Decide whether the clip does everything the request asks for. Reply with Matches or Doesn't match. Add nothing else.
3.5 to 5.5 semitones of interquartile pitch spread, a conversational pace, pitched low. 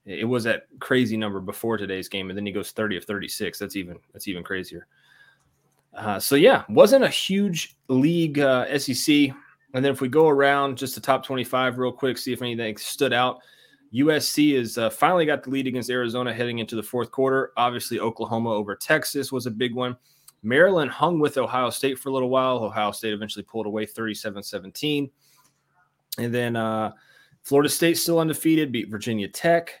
Matches